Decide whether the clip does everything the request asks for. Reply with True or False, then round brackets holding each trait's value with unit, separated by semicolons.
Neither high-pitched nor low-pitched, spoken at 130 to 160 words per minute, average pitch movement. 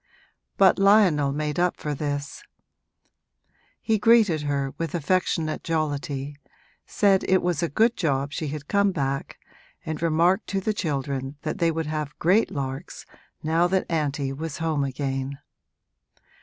True (155 Hz; 140 wpm; 4.1 semitones)